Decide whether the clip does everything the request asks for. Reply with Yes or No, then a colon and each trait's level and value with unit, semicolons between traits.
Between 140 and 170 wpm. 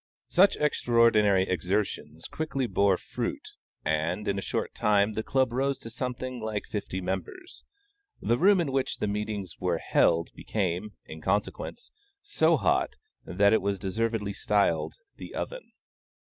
Yes: average, 145 wpm